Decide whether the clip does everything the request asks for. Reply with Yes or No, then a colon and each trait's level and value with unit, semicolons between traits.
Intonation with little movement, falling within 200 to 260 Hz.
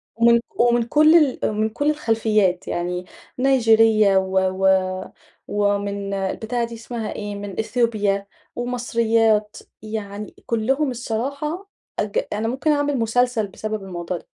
No: average, 3.2 semitones; high, 220 Hz